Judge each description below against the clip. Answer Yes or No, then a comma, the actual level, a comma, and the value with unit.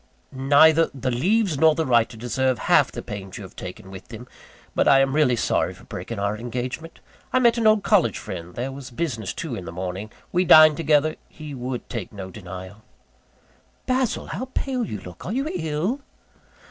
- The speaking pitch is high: No, low, 130 Hz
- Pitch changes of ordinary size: No, wide, 7.2 semitones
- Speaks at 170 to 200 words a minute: Yes, average, 190 wpm